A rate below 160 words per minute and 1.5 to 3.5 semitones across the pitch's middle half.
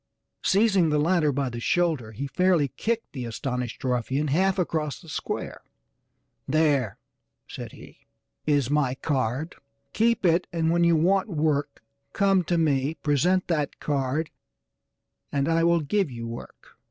No: average, 145 wpm; average, 4.3 semitones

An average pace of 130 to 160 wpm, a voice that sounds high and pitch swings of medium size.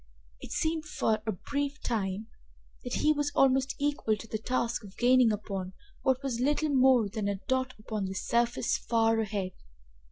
No: average, 170 wpm; high, 235 Hz; average, 3.9 semitones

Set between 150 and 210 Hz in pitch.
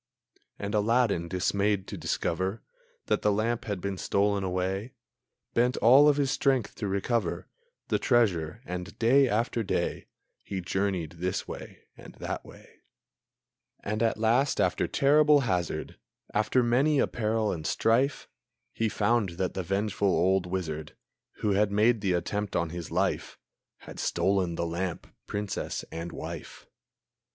No: low, 100 Hz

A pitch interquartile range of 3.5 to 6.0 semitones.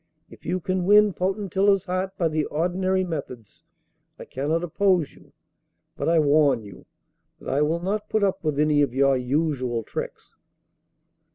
Yes: average, 4.8 semitones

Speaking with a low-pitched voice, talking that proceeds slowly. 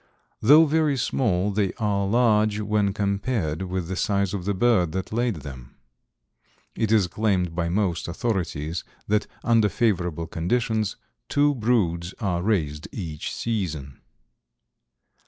Yes: low, 100 Hz; slow, 130 wpm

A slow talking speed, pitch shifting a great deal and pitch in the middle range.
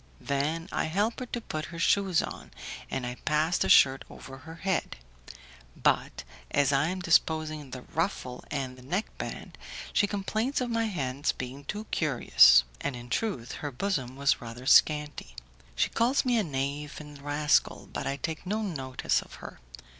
No: average, 175 wpm; wide, 6.0 semitones; medium, 150 Hz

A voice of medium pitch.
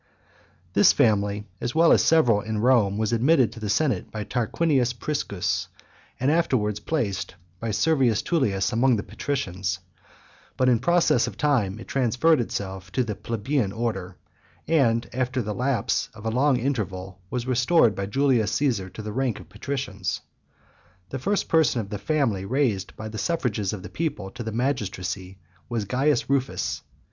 No: low, 115 Hz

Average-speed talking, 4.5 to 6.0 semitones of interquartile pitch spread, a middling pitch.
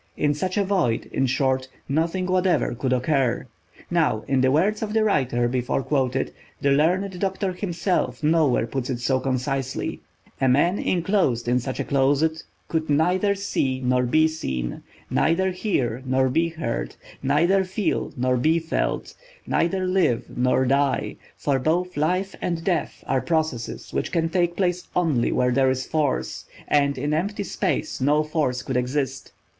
Yes: average, 160 wpm; average, 5.3 semitones; medium, 150 Hz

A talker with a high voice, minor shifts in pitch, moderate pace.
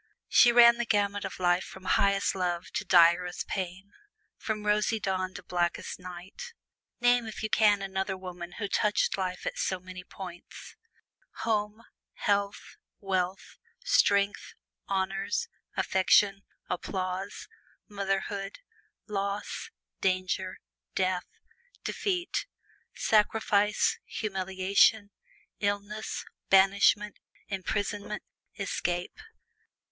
No: high, 195 Hz; narrow, 2.1 semitones; slow, 100 wpm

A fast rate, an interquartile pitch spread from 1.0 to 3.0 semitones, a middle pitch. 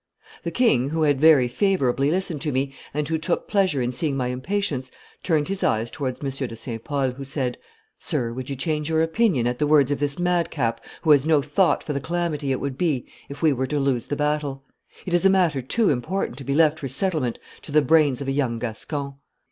No: fast, 230 wpm; average, 3.7 semitones; medium, 145 Hz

